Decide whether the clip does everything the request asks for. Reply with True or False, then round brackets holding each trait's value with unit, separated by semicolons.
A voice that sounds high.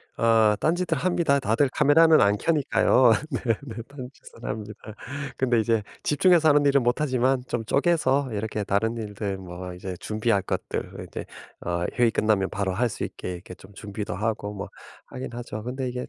False (115 Hz)